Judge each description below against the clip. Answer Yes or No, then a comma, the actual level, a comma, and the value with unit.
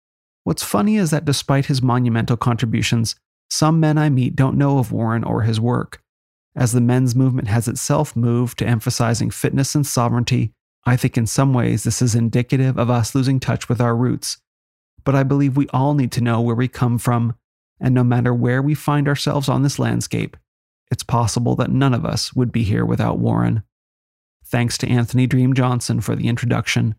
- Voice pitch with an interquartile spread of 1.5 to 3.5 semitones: Yes, narrow, 2.5 semitones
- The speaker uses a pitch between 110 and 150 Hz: Yes, low, 125 Hz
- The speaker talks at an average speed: Yes, average, 195 wpm